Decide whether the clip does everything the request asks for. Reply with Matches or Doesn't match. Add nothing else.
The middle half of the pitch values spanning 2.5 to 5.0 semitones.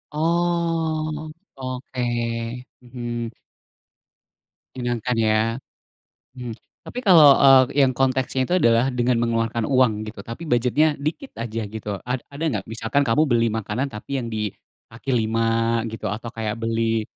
Matches